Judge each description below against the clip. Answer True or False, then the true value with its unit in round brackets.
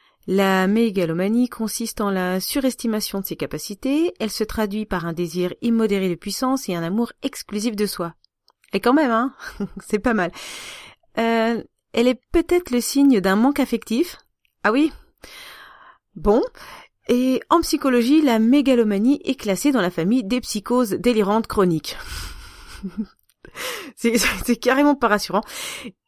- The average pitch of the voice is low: False (230 Hz)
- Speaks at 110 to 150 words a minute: True (145 wpm)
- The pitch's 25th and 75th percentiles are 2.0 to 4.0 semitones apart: False (4.5 semitones)